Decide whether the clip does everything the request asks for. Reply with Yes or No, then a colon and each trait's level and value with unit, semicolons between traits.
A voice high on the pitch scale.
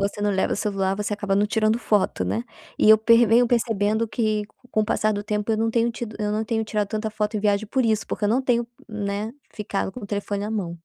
Yes: high, 215 Hz